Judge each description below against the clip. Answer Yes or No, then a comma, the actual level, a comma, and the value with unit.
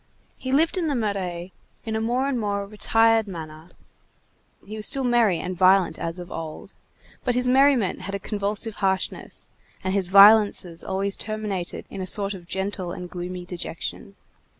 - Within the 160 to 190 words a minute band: Yes, average, 170 wpm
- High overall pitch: Yes, high, 200 Hz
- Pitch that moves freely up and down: No, average, 3.5 semitones